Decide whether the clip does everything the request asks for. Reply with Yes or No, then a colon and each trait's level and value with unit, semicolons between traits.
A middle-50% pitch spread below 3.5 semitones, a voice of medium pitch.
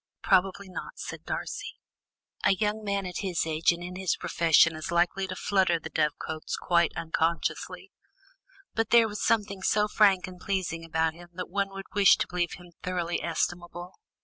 Yes: narrow, 2.6 semitones; medium, 180 Hz